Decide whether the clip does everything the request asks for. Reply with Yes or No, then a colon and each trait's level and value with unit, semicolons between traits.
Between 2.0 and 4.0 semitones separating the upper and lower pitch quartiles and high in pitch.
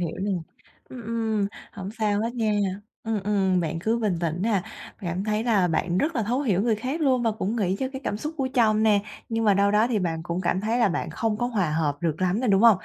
Yes: average, 3.7 semitones; high, 210 Hz